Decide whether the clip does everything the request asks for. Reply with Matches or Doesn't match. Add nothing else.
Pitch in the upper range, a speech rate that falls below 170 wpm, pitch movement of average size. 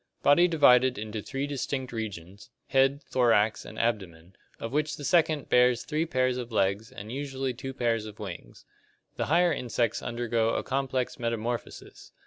Doesn't match